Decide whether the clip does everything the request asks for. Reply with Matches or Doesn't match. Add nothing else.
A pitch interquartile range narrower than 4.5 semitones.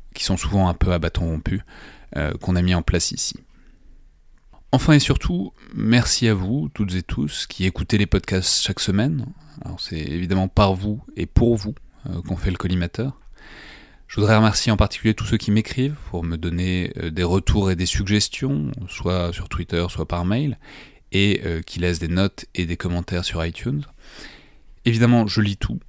Matches